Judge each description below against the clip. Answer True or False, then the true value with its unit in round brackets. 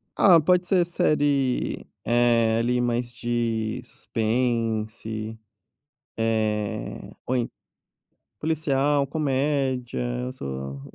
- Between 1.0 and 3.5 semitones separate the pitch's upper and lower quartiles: False (3.9 semitones)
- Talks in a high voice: False (120 Hz)